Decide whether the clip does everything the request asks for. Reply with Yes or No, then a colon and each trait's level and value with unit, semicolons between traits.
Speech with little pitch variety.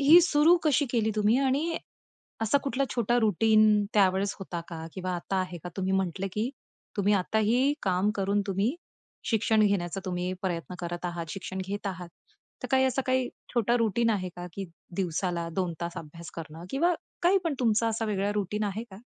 No: average, 4.4 semitones